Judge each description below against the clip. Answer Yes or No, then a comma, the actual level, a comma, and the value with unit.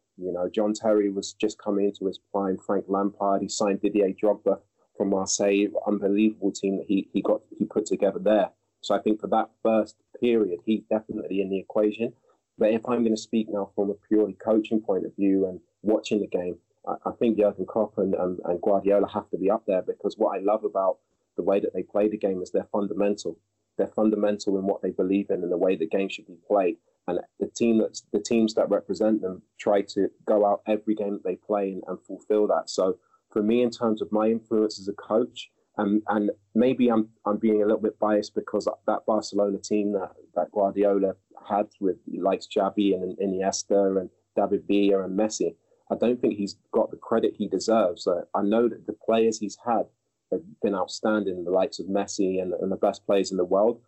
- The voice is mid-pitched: No, low, 105 Hz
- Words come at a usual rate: No, fast, 220 wpm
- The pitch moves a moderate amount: No, narrow, 1.7 semitones